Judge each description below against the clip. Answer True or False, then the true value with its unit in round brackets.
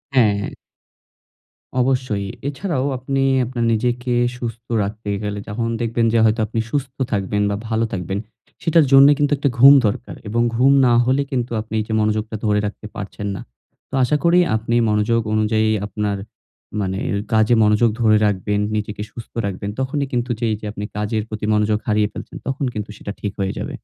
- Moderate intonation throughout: True (3.0 semitones)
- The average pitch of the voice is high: False (110 Hz)